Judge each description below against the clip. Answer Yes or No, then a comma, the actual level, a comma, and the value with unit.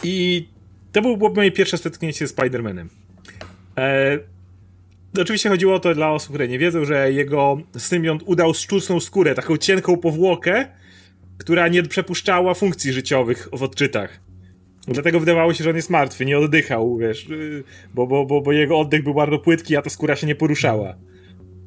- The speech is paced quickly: Yes, fast, 165 wpm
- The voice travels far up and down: Yes, wide, 7.7 semitones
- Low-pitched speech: No, medium, 145 Hz